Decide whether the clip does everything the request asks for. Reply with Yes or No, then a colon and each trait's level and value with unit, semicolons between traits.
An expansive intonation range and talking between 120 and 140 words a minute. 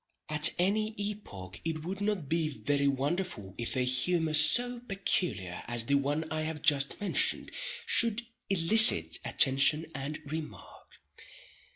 Yes: wide, 5.8 semitones; slow, 135 wpm